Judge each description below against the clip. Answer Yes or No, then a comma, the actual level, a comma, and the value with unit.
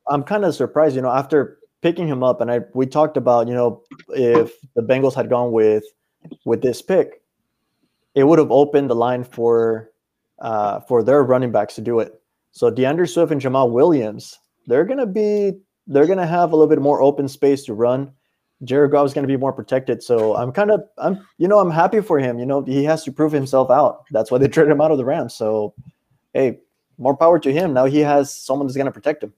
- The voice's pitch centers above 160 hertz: No, medium, 140 Hz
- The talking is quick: Yes, fast, 225 wpm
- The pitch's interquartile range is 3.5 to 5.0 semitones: Yes, average, 3.9 semitones